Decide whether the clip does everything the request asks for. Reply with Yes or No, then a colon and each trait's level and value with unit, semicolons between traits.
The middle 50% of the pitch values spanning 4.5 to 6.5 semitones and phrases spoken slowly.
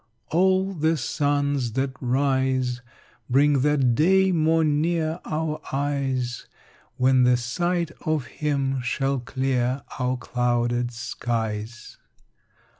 No: average, 3.8 semitones; slow, 105 wpm